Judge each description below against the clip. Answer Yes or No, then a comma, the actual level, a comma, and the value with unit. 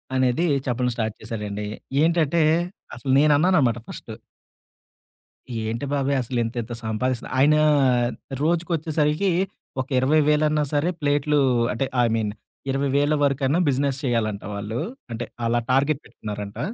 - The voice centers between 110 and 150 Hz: Yes, low, 135 Hz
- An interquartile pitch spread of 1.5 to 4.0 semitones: No, average, 4.6 semitones